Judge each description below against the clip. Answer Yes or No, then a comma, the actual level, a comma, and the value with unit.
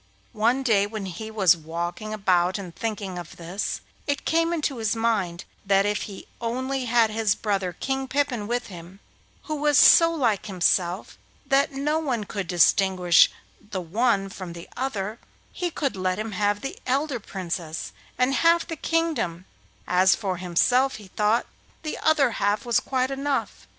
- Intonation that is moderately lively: No, wide, 6.1 semitones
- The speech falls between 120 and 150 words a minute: No, average, 165 wpm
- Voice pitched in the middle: No, high, 215 Hz